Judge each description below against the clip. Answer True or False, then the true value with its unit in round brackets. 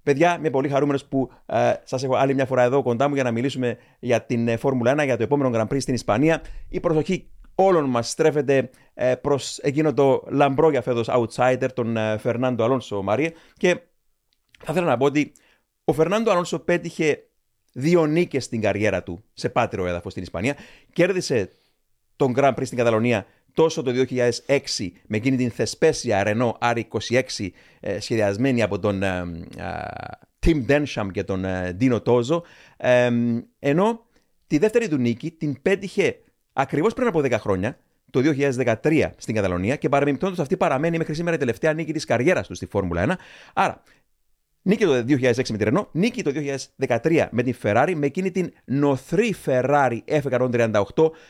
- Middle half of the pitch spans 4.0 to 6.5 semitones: True (5.1 semitones)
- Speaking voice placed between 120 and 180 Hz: True (130 Hz)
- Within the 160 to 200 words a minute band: True (165 wpm)